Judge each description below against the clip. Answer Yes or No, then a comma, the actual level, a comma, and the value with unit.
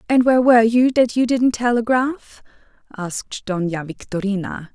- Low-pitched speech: No, high, 225 Hz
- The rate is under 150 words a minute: Yes, average, 140 wpm